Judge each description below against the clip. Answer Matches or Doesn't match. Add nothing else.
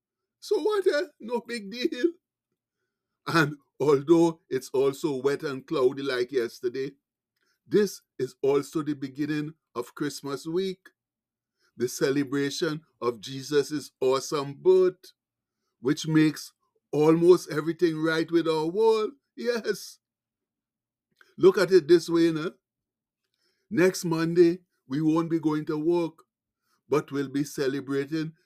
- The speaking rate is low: Matches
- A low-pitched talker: Doesn't match